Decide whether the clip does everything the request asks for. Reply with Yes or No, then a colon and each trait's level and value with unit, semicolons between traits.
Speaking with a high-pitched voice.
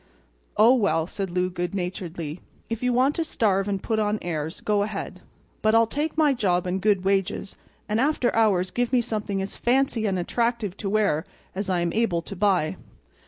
Yes: high, 205 Hz